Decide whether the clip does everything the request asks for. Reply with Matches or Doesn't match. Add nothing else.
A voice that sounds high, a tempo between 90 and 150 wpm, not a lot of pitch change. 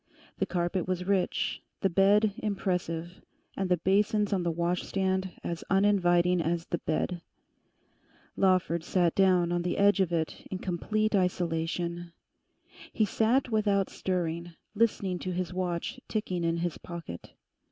Doesn't match